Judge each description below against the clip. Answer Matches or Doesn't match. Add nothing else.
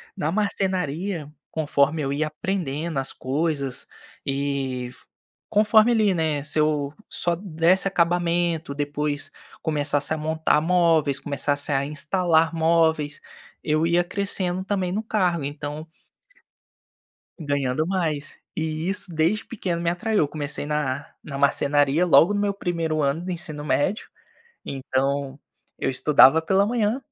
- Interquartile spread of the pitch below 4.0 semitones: Matches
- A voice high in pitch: Doesn't match